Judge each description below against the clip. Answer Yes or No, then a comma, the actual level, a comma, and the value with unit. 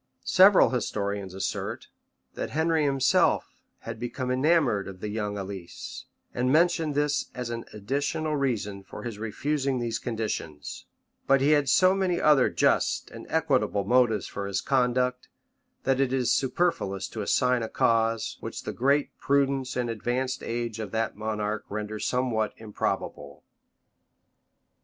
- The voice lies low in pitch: Yes, low, 125 Hz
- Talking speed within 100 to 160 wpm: Yes, average, 140 wpm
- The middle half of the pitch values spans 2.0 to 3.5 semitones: No, average, 4.5 semitones